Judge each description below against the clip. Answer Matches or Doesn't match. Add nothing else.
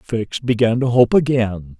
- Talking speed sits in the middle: Matches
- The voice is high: Doesn't match